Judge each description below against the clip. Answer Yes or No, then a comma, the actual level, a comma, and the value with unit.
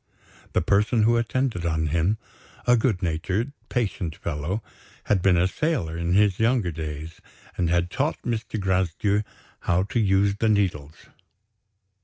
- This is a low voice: Yes, very low, 95 Hz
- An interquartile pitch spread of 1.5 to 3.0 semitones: No, average, 4.6 semitones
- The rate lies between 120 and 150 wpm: Yes, average, 145 wpm